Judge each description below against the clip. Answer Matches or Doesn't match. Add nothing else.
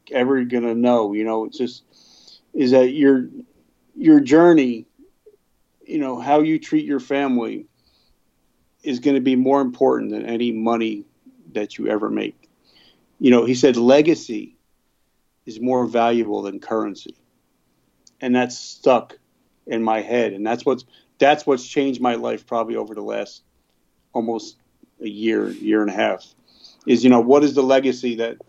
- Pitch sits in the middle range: Doesn't match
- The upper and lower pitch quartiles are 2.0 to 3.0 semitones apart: Doesn't match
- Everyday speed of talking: Matches